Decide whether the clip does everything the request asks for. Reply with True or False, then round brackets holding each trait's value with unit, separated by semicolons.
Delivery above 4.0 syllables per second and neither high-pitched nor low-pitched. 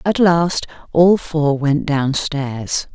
False (2.7 syllables/s; 155 Hz)